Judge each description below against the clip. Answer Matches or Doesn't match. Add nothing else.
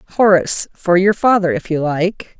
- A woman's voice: Matches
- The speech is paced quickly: Doesn't match